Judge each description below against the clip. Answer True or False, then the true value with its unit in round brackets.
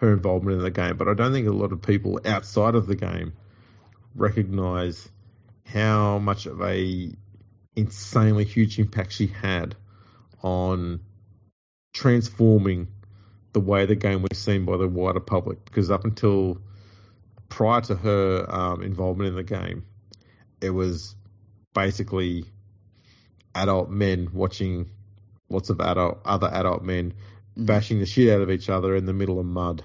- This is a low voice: True (100 Hz)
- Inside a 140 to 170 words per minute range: True (150 wpm)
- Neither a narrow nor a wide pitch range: False (2.1 semitones)